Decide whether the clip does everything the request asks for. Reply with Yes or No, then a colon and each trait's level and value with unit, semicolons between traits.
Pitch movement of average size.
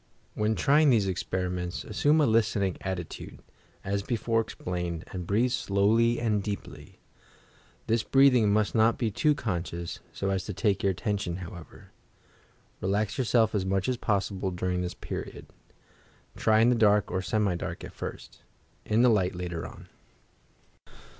Yes: average, 3.6 semitones